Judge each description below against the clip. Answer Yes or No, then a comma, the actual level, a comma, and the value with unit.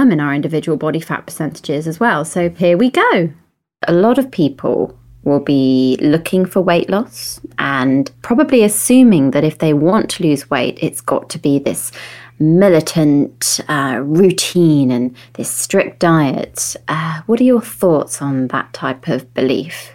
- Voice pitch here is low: No, medium, 155 Hz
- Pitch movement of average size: Yes, average, 4.7 semitones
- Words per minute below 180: Yes, average, 160 wpm